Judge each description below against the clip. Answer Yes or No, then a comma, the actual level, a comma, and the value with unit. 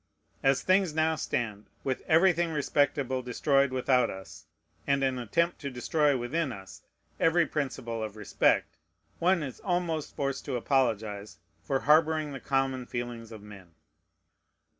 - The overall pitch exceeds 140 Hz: No, low, 135 Hz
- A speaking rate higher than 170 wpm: No, average, 140 wpm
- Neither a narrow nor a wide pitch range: Yes, average, 4.6 semitones